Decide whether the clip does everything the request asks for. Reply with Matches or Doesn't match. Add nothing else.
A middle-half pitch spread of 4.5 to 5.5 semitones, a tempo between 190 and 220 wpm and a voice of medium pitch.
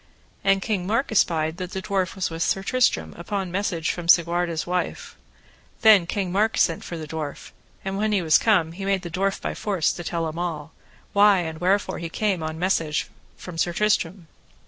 Doesn't match